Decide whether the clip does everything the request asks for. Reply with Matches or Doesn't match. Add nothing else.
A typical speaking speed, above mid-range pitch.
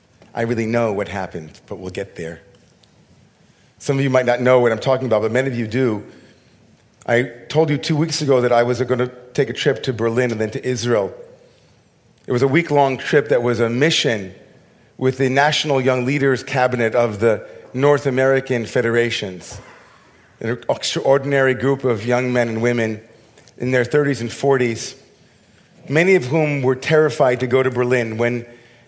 Doesn't match